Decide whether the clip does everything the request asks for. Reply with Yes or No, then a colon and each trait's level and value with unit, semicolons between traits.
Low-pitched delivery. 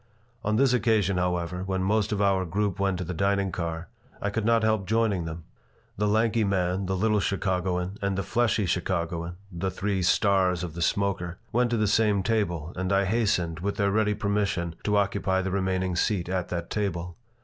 Yes: very low, 95 Hz